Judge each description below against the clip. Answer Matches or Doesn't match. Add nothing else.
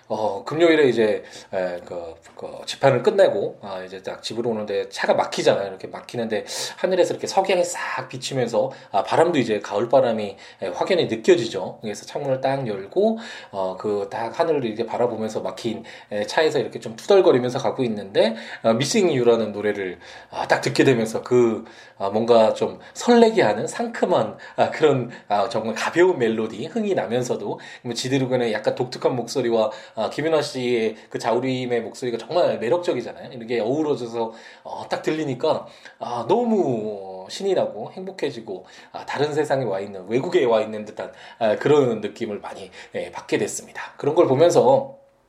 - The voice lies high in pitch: Doesn't match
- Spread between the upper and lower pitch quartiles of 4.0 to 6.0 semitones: Doesn't match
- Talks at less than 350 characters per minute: Doesn't match